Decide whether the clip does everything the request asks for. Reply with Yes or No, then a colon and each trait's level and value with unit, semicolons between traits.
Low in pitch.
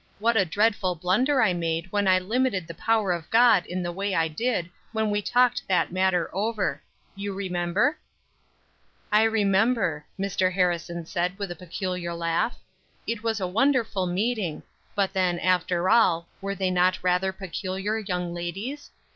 No: high, 190 Hz